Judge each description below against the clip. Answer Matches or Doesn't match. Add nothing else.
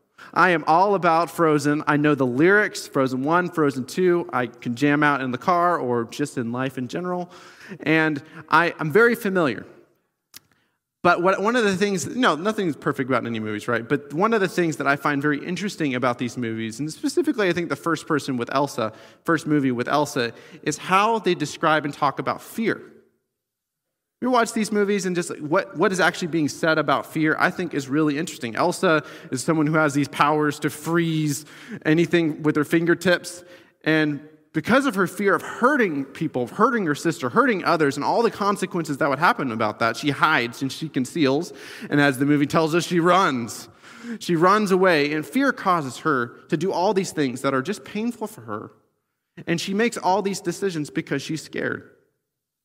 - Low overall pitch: Doesn't match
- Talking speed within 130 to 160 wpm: Doesn't match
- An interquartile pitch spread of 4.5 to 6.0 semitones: Doesn't match